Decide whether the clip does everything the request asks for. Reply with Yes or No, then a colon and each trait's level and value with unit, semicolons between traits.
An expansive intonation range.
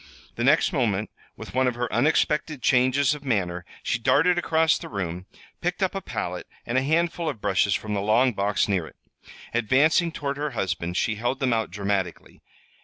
Yes: wide, 5.9 semitones